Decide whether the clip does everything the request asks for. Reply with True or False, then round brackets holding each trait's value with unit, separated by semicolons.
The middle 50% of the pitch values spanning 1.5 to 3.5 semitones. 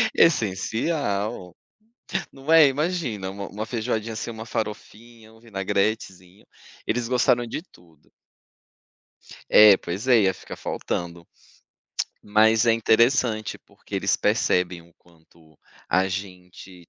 False (4.1 semitones)